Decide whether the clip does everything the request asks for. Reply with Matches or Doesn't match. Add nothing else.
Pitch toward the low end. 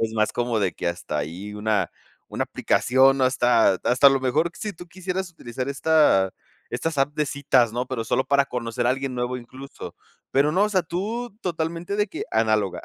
Matches